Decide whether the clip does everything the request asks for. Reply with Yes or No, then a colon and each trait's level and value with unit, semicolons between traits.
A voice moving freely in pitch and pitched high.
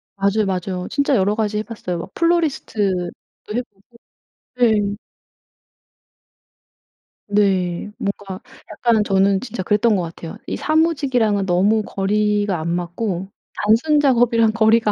No: average, 3.2 semitones; high, 210 Hz